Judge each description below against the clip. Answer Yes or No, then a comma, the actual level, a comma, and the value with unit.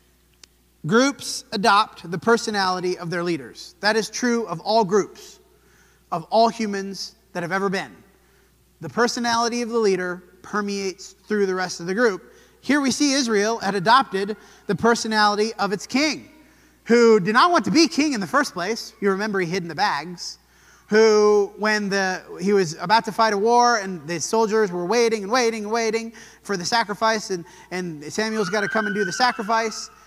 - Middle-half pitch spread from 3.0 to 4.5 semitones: Yes, average, 3.3 semitones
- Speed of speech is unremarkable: Yes, average, 185 wpm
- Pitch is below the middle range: No, high, 210 Hz